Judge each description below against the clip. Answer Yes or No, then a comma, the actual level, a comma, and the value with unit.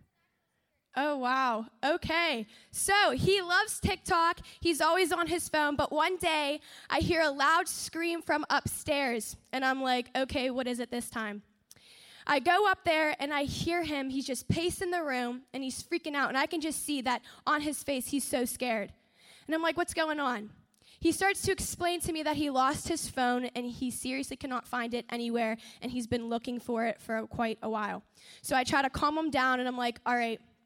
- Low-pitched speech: No, very high, 275 Hz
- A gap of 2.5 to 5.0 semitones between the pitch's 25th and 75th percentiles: Yes, average, 4.6 semitones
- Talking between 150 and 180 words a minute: No, fast, 205 wpm